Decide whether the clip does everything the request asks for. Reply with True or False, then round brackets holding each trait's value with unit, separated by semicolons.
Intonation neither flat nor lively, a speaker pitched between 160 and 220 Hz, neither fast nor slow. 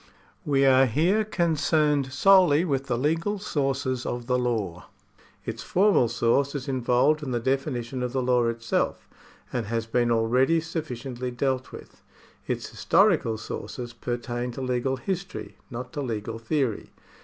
False (3.7 semitones; 130 Hz; 145 wpm)